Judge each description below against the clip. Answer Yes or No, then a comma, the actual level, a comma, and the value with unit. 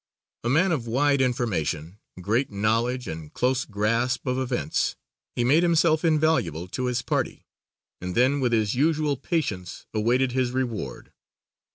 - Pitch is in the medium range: No, low, 125 Hz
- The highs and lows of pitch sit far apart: No, average, 4.5 semitones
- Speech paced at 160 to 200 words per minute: No, average, 145 wpm